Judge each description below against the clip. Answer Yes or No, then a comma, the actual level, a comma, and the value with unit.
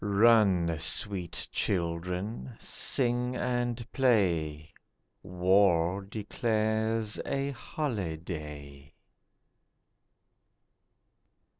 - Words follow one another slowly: Yes, slow, 50 wpm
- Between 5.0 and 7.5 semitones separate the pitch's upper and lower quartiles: Yes, wide, 5.6 semitones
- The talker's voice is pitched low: Yes, low, 100 Hz